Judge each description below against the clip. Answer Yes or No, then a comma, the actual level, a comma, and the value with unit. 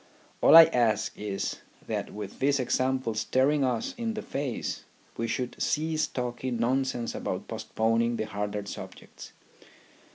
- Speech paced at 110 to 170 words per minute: Yes, slow, 135 wpm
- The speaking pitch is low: Yes, low, 125 Hz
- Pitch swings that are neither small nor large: Yes, average, 3.8 semitones